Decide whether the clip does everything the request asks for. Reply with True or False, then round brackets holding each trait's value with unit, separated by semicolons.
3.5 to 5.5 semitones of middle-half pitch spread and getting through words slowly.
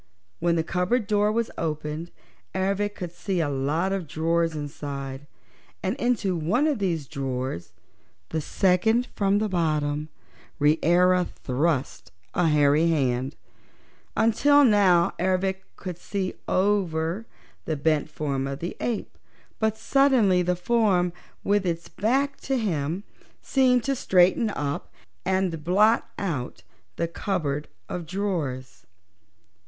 True (5.2 semitones; 125 wpm)